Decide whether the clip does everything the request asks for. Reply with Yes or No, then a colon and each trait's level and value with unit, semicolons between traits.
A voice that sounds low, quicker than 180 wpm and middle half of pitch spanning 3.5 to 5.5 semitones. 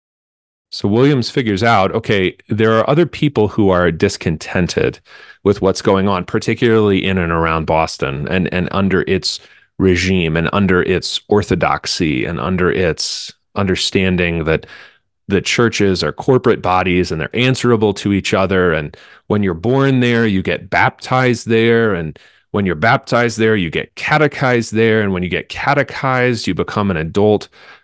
No: low, 100 Hz; average, 155 wpm; average, 4.1 semitones